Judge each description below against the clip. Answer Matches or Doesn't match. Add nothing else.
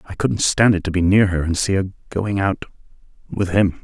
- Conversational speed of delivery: Doesn't match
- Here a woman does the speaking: Doesn't match